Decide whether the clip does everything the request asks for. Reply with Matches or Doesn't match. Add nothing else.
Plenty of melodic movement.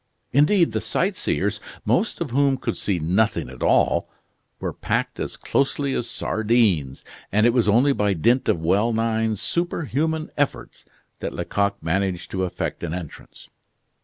Matches